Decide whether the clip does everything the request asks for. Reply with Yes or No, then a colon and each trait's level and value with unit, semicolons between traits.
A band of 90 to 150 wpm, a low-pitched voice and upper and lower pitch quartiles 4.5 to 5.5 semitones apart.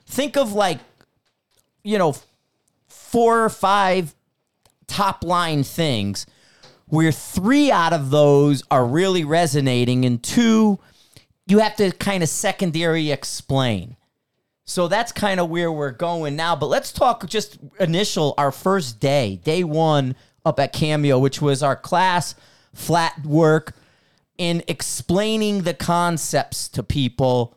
No: slow, 135 wpm; medium, 160 Hz; average, 5.2 semitones